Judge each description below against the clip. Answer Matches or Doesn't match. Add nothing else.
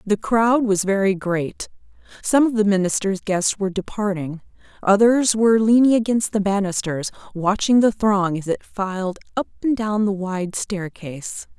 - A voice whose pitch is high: Matches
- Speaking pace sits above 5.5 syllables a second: Doesn't match